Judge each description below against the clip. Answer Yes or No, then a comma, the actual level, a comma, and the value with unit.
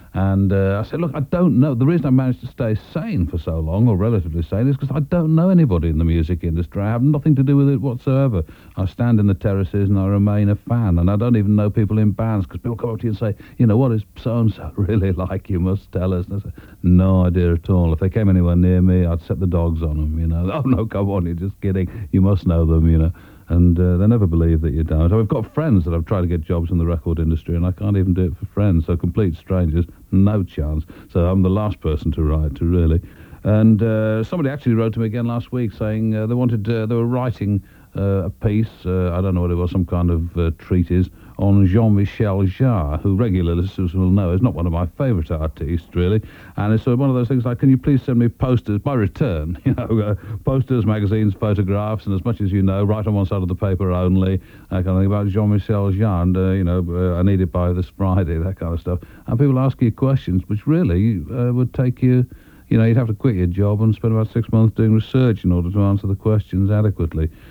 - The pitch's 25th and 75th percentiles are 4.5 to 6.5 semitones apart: No, average, 4.1 semitones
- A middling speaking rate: No, fast, 265 wpm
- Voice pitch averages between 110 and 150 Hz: No, low, 100 Hz